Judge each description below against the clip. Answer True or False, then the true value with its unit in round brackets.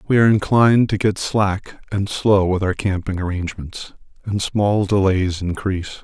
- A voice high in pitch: False (100 Hz)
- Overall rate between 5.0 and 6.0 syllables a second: False (4.8 syllables/s)